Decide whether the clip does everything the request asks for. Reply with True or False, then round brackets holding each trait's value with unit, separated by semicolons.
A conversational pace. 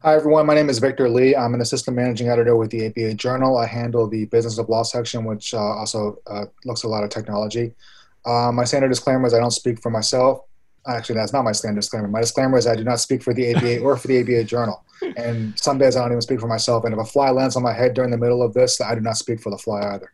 False (280 wpm)